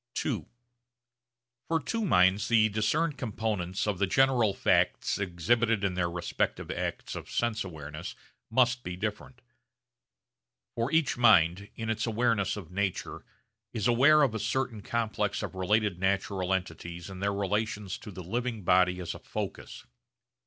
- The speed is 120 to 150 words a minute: Yes, average, 145 wpm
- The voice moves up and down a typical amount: Yes, average, 4.1 semitones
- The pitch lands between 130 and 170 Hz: No, low, 105 Hz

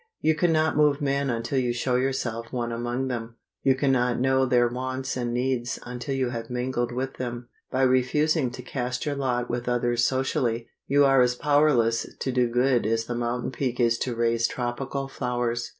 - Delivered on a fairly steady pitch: Yes, narrow, 1.8 semitones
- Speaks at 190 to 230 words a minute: Yes, average, 195 wpm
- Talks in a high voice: No, low, 125 Hz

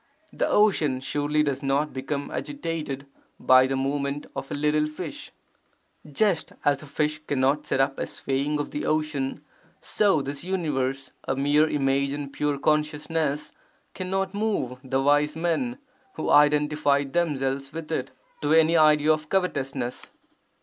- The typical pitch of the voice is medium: Yes, medium, 150 Hz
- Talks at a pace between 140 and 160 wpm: Yes, average, 145 wpm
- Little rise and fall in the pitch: Yes, narrow, 2.2 semitones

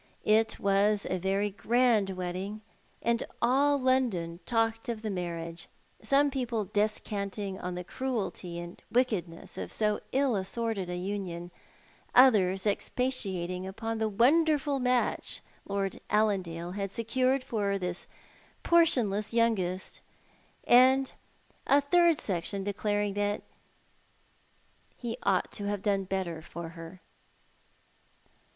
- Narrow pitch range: No, average, 4.3 semitones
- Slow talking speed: Yes, slow, 115 wpm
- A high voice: Yes, high, 205 Hz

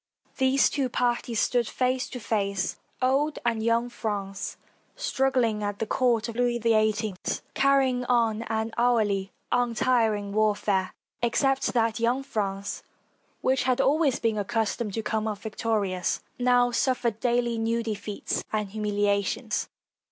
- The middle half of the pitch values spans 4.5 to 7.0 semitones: No, average, 2.7 semitones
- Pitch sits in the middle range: No, high, 230 Hz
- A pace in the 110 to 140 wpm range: Yes, slow, 135 wpm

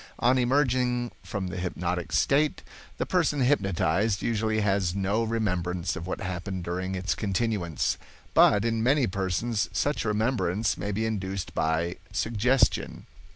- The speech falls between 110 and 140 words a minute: Yes, slow, 135 wpm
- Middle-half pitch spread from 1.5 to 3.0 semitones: No, average, 4.2 semitones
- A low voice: Yes, low, 105 Hz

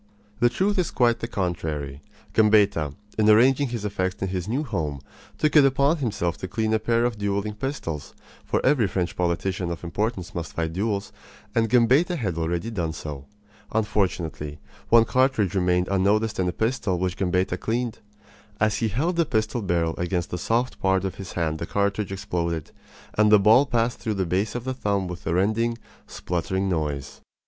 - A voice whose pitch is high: No, low, 100 Hz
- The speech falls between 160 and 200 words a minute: Yes, average, 180 wpm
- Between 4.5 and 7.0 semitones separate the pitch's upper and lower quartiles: Yes, average, 4.8 semitones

